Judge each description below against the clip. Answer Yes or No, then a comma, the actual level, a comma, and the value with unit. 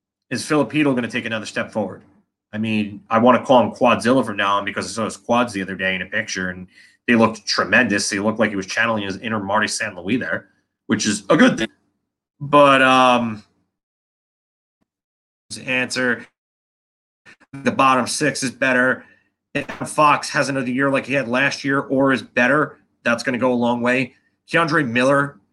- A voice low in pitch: Yes, low, 120 Hz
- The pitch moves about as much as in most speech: Yes, average, 4.7 semitones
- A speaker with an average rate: Yes, average, 195 wpm